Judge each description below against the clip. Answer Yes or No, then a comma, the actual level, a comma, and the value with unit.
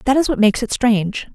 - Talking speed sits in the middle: No, fast, 270 wpm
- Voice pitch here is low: No, high, 235 Hz